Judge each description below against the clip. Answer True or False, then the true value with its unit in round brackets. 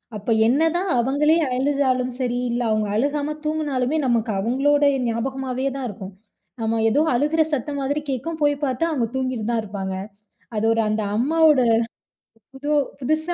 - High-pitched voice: True (260 Hz)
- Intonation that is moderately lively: True (4.0 semitones)